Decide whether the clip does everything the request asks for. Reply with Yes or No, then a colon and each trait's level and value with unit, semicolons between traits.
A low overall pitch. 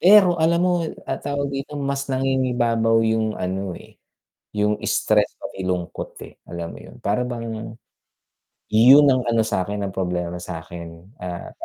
Yes: low, 110 Hz